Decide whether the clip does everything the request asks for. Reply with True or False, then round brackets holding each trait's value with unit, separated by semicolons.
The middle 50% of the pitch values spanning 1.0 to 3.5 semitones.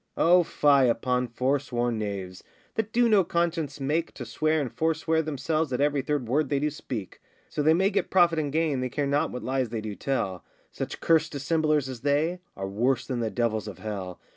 False (4.8 semitones)